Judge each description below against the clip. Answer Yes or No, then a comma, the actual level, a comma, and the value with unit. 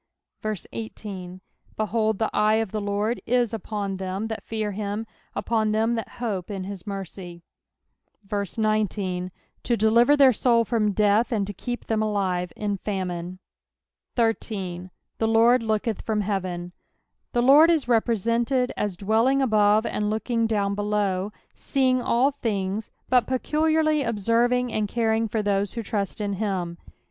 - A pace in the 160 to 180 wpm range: No, average, 145 wpm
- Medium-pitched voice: No, high, 215 Hz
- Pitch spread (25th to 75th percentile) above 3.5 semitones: No, average, 2.8 semitones